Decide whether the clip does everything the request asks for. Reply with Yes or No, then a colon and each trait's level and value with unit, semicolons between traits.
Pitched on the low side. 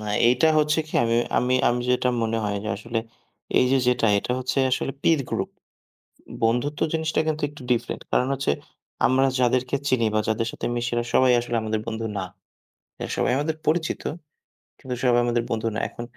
Yes: low, 125 Hz